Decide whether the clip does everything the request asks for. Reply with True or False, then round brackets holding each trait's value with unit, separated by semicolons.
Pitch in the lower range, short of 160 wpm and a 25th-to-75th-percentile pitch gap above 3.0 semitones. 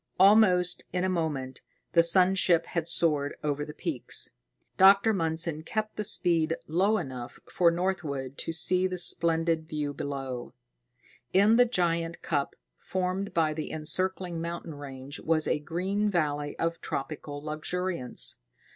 False (165 Hz; 140 wpm; 3.5 semitones)